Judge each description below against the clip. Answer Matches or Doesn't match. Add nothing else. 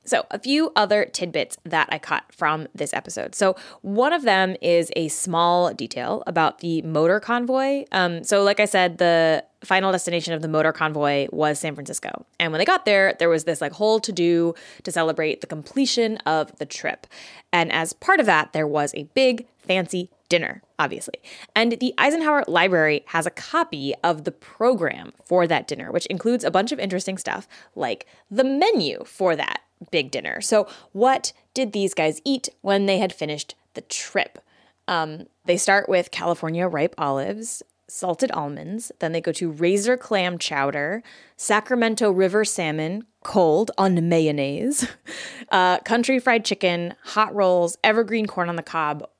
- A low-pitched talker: Doesn't match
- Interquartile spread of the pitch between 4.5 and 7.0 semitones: Matches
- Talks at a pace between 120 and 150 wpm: Doesn't match